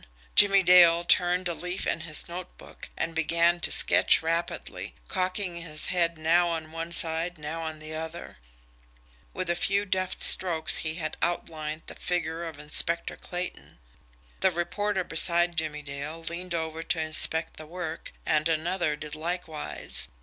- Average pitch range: No, narrow, 1.9 semitones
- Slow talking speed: No, average, 155 wpm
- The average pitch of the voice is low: No, medium, 165 Hz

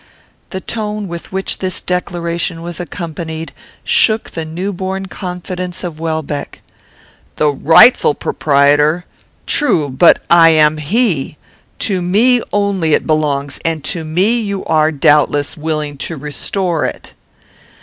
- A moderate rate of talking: No, slow, 130 wpm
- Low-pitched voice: No, medium, 170 Hz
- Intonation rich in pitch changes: No, average, 3.6 semitones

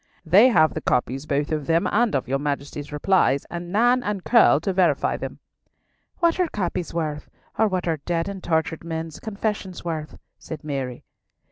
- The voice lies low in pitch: No, medium, 165 Hz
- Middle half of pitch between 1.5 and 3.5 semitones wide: No, average, 4.9 semitones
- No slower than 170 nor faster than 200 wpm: Yes, average, 175 wpm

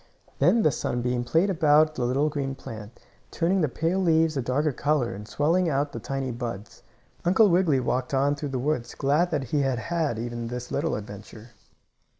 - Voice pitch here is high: No, medium, 140 Hz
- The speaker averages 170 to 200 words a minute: Yes, average, 185 wpm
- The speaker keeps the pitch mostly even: No, average, 4.6 semitones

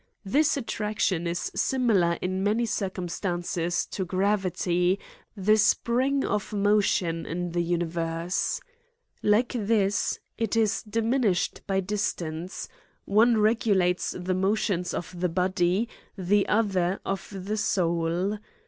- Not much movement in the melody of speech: No, average, 3.2 semitones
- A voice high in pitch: Yes, high, 195 Hz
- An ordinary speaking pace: No, slow, 115 wpm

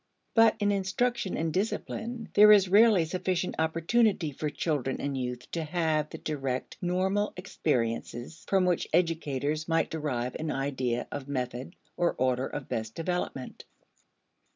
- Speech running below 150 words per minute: Yes, average, 140 wpm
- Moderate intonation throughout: No, wide, 5.7 semitones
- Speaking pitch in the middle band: Yes, medium, 160 Hz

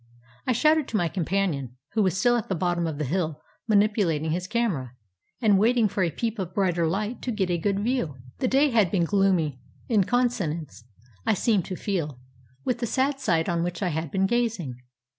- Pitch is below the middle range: No, high, 190 Hz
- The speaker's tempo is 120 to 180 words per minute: No, average, 200 wpm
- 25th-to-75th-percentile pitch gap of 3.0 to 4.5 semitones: No, average, 5.3 semitones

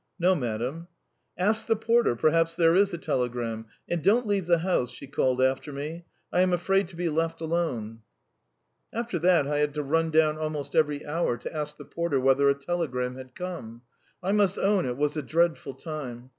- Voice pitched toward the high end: No, medium, 155 Hz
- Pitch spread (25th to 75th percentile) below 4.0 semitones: No, average, 4.5 semitones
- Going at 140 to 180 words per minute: No, average, 195 wpm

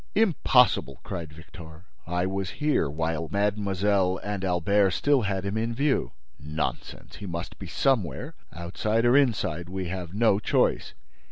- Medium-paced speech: Yes, average, 145 wpm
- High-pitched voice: No, very low, 95 Hz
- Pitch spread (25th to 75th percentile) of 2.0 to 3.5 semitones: No, average, 4.2 semitones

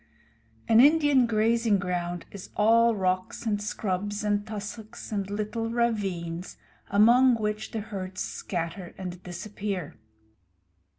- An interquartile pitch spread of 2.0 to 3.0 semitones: No, average, 3.5 semitones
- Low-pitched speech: No, high, 205 Hz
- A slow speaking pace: Yes, slow, 115 wpm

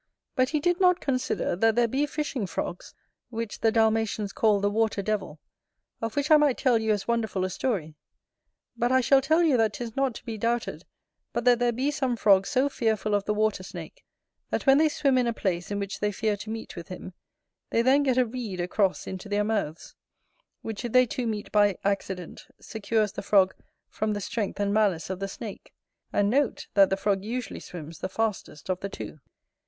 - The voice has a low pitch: No, high, 220 Hz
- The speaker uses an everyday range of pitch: Yes, average, 3.9 semitones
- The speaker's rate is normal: No, fast, 210 wpm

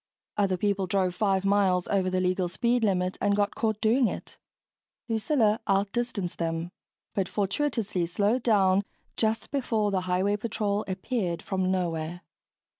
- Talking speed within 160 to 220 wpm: No, average, 145 wpm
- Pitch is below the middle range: No, high, 200 Hz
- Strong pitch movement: No, average, 2.8 semitones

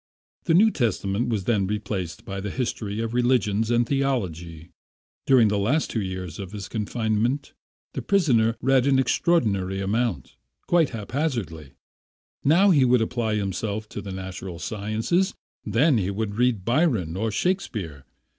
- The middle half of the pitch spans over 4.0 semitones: Yes, average, 4.7 semitones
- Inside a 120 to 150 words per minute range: Yes, average, 145 wpm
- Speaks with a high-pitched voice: No, low, 110 Hz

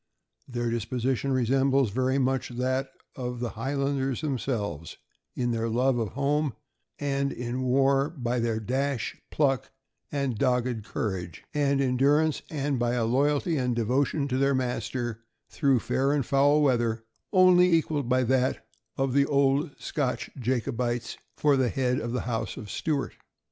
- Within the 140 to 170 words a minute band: Yes, average, 155 wpm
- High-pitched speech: No, low, 130 Hz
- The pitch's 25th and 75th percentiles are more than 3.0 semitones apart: No, narrow, 2.5 semitones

